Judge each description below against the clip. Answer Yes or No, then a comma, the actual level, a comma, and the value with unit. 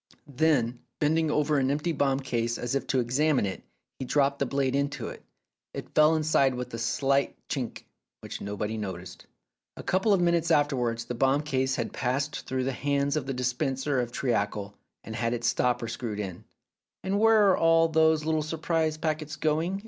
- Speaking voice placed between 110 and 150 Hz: Yes, medium, 140 Hz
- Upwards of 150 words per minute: Yes, average, 185 wpm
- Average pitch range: Yes, average, 4.1 semitones